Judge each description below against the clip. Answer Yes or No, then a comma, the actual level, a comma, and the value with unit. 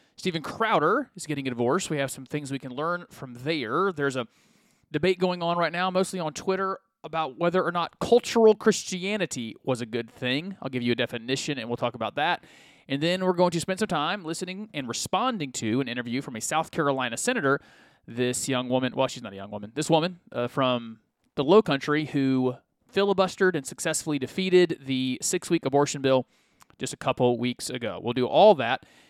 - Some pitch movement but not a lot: No, wide, 6.1 semitones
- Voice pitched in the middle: Yes, medium, 150 Hz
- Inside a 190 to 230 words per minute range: Yes, average, 200 wpm